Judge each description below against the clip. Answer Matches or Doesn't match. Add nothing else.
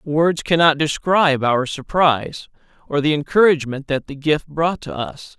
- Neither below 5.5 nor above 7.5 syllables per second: Doesn't match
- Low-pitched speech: Doesn't match